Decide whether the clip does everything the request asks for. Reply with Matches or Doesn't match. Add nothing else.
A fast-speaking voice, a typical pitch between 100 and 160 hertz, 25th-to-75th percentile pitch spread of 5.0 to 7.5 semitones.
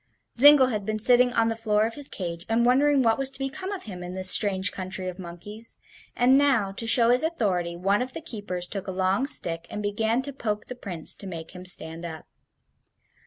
Doesn't match